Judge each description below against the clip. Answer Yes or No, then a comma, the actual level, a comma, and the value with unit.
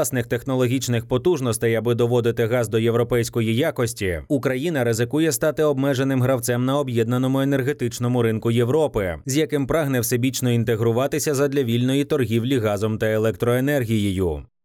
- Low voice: Yes, low, 125 Hz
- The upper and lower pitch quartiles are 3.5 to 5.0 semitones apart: No, average, 3.0 semitones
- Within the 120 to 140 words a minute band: Yes, average, 125 wpm